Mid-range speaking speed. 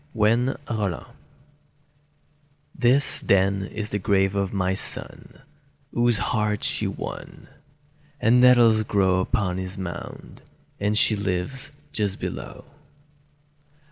No: slow, 110 wpm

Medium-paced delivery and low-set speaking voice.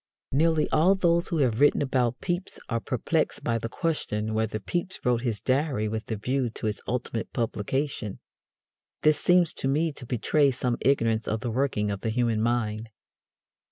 Yes: average, 175 wpm; low, 125 Hz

